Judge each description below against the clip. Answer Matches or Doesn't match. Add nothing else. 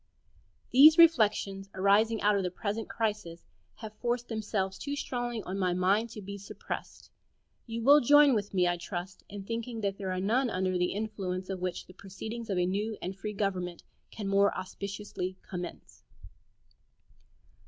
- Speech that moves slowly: Doesn't match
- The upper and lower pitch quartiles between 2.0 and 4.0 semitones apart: Matches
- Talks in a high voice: Matches